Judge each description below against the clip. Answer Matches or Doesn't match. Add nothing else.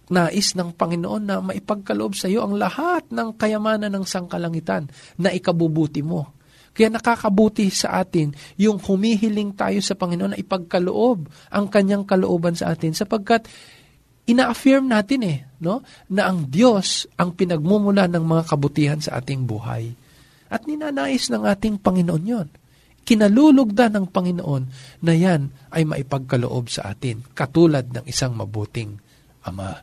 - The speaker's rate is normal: Matches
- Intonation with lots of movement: Matches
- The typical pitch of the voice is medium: Matches